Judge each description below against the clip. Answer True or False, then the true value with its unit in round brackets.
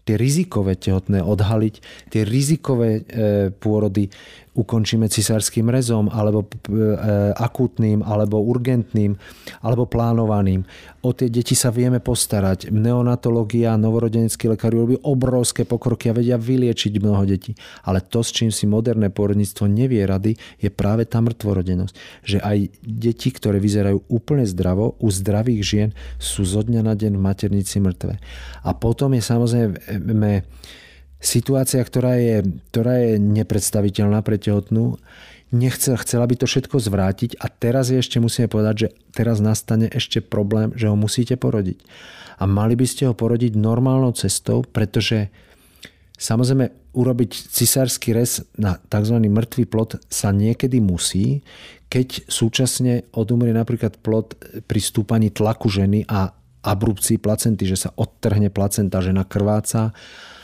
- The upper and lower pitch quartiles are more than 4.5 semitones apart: False (2.6 semitones)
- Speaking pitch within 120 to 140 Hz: False (110 Hz)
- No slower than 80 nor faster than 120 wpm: False (135 wpm)